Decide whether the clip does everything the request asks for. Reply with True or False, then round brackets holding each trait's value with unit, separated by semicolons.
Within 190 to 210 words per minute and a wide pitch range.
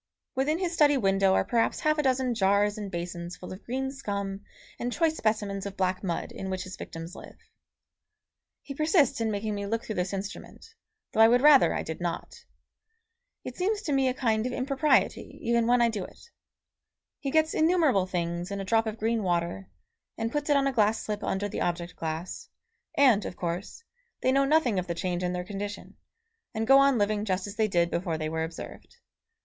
True (205 wpm; 6.0 semitones)